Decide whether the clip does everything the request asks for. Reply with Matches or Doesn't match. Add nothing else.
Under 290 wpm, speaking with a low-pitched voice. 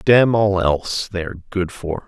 Matches